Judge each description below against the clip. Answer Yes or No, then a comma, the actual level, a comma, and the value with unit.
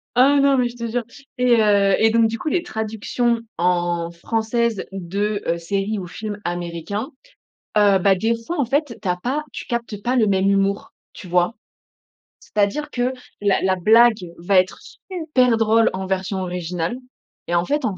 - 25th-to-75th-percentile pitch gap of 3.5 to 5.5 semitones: Yes, average, 4.2 semitones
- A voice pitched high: Yes, high, 210 Hz